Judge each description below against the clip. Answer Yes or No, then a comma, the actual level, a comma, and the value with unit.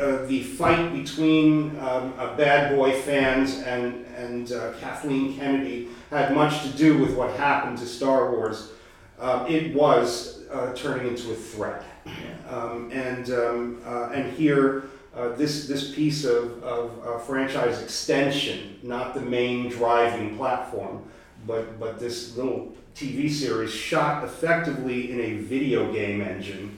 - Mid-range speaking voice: No, low, 125 Hz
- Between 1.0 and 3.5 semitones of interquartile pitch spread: Yes, average, 2.8 semitones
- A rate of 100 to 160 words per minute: Yes, average, 145 wpm